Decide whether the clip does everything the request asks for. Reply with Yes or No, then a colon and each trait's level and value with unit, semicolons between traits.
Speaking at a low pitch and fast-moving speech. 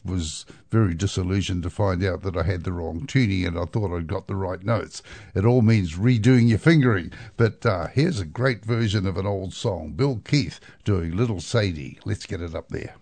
Yes: low, 100 Hz; fast, 210 wpm